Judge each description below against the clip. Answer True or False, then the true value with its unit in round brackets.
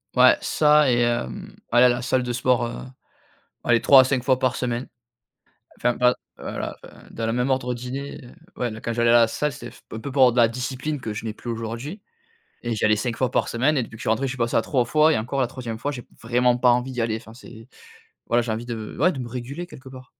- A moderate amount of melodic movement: False (1.8 semitones)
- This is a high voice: False (125 Hz)